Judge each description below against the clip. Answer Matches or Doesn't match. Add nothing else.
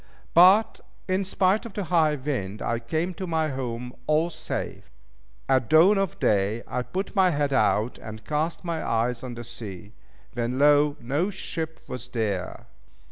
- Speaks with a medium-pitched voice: Matches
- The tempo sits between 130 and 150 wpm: Doesn't match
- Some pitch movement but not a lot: Doesn't match